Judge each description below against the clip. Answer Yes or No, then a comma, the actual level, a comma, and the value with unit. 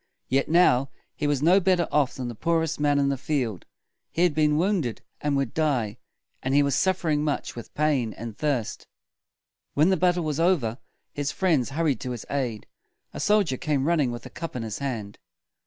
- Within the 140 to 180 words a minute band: No, fast, 205 wpm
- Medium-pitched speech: Yes, medium, 145 Hz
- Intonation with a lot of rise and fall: No, average, 4.5 semitones